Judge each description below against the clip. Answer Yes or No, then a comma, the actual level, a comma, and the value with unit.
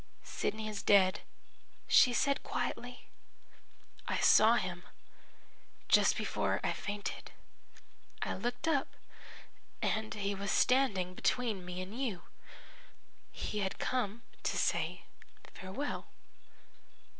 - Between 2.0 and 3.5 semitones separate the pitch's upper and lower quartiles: No, average, 4.4 semitones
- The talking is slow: Yes, slow, 105 wpm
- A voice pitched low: No, high, 215 Hz